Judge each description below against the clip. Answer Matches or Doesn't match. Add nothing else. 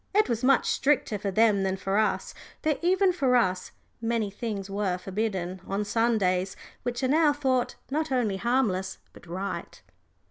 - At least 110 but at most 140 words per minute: Doesn't match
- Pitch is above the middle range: Matches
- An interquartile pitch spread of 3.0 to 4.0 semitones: Doesn't match